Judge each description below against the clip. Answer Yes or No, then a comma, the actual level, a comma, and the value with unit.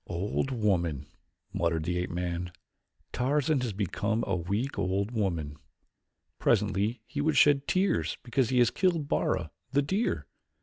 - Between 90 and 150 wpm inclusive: Yes, average, 140 wpm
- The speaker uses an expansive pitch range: Yes, wide, 7.4 semitones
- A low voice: Yes, low, 105 Hz